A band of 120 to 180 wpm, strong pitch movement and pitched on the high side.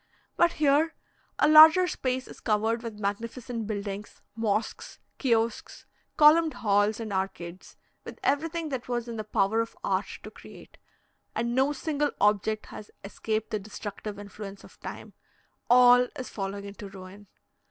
No: average, 145 wpm; average, 4.2 semitones; high, 225 Hz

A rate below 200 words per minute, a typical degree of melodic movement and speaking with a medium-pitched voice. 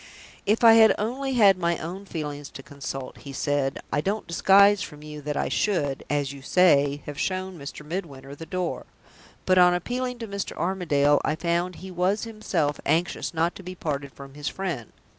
Yes: average, 190 wpm; average, 5.0 semitones; medium, 170 Hz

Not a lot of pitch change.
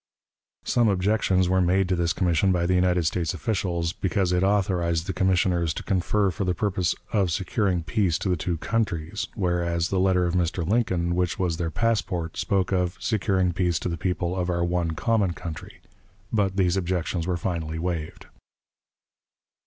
Yes: narrow, 1.9 semitones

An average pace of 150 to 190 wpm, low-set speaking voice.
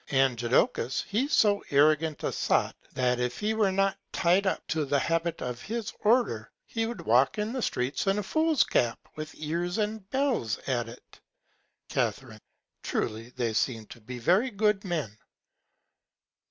No: average, 165 wpm; medium, 165 Hz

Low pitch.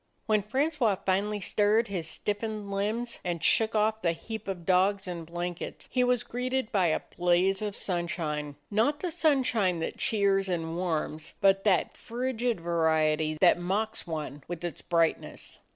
No: high, 195 Hz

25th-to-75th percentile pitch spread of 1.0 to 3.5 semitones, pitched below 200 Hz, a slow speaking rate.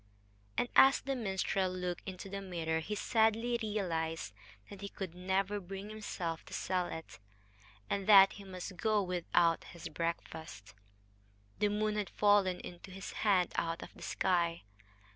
No: average, 3.1 semitones; high, 190 Hz; average, 155 wpm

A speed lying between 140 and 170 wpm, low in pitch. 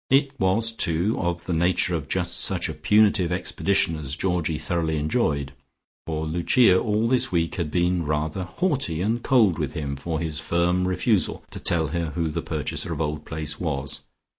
No: average, 180 wpm; very low, 85 Hz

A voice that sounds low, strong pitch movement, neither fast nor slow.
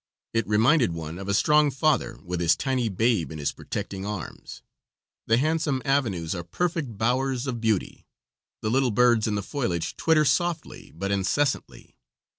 Yes: low, 115 Hz; wide, 6.0 semitones; average, 160 wpm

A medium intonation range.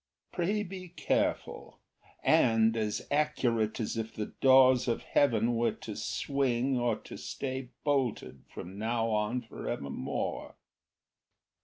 Yes: average, 3.5 semitones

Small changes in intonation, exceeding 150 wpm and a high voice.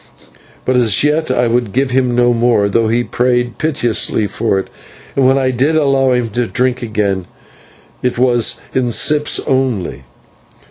No: narrow, 2.1 semitones; average, 165 wpm; low, 125 Hz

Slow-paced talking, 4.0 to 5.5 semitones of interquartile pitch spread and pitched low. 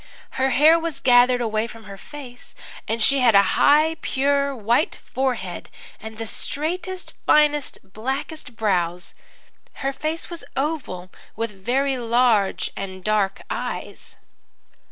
No: slow, 130 wpm; average, 5.0 semitones; high, 245 Hz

